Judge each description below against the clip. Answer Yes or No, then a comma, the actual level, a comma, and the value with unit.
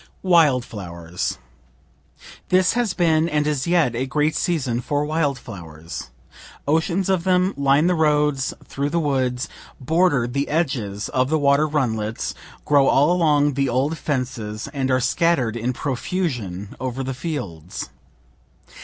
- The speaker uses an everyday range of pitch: Yes, average, 4.5 semitones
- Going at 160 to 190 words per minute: No, average, 140 wpm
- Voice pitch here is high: No, medium, 140 Hz